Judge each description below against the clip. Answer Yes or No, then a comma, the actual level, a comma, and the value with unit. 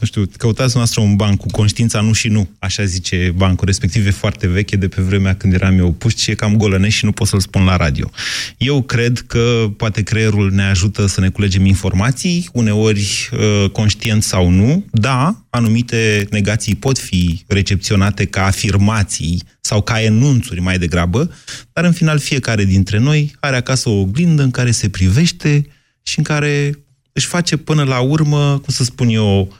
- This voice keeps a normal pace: No, fast, 180 wpm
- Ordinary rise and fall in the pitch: Yes, average, 4.6 semitones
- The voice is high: No, low, 110 Hz